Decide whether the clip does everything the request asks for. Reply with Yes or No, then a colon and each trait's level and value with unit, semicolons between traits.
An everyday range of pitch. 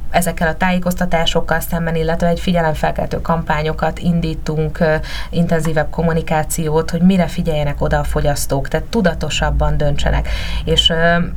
No: narrow, 1.5 semitones